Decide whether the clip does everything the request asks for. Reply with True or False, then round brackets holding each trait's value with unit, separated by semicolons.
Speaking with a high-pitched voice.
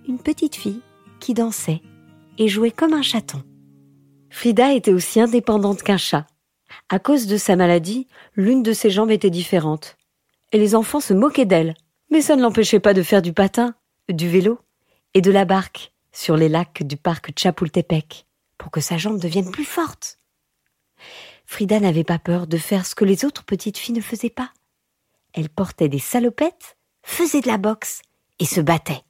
True (200 Hz)